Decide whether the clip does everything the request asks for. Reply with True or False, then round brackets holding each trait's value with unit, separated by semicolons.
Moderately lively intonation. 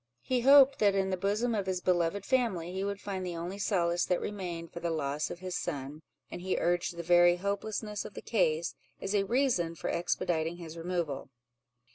True (3.0 semitones)